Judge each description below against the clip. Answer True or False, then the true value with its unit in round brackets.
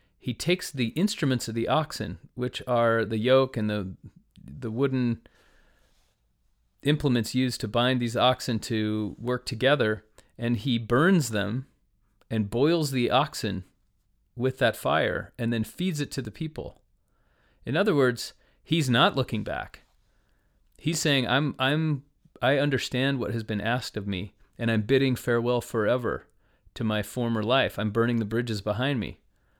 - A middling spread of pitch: True (3.7 semitones)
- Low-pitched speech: True (120 Hz)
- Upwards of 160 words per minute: False (155 wpm)